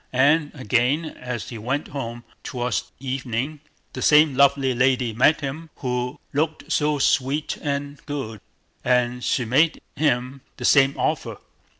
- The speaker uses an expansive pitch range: No, average, 2.9 semitones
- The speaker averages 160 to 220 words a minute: No, slow, 135 wpm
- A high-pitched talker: No, low, 135 Hz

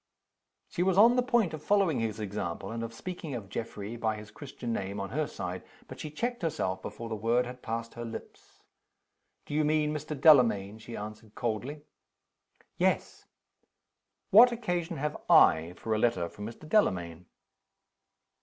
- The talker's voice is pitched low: Yes, low, 120 Hz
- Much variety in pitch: Yes, wide, 6.6 semitones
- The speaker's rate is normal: Yes, average, 165 wpm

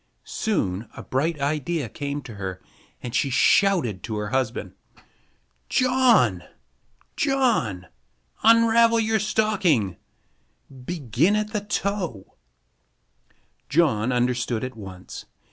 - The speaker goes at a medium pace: No, slow, 100 wpm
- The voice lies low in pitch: No, medium, 145 Hz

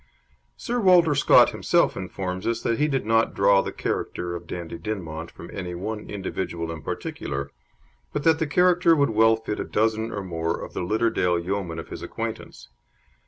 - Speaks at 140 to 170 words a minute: No, average, 180 wpm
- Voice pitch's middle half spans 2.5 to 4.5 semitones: No, average, 5.1 semitones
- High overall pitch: No, low, 100 Hz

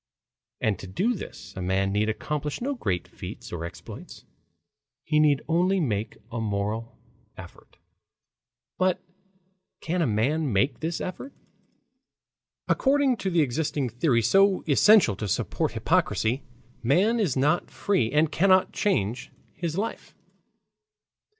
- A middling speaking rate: No, slow, 130 wpm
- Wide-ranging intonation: Yes, wide, 8.9 semitones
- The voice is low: No, medium, 150 Hz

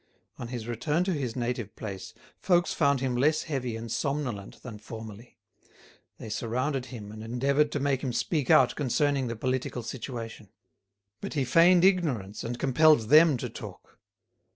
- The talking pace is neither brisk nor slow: Yes, average, 160 wpm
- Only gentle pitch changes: No, average, 4.1 semitones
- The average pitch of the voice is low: Yes, low, 125 Hz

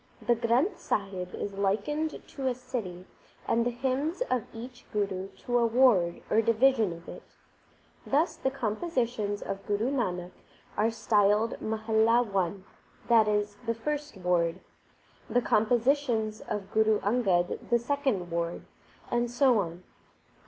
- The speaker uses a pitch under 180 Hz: No, high, 225 Hz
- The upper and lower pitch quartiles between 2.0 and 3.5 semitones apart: No, average, 3.9 semitones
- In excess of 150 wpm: No, average, 140 wpm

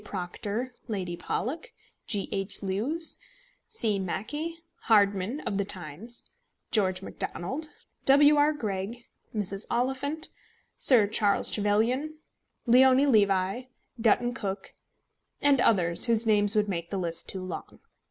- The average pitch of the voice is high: Yes, high, 215 Hz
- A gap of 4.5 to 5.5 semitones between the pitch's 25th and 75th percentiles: Yes, average, 5.0 semitones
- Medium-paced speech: No, slow, 120 wpm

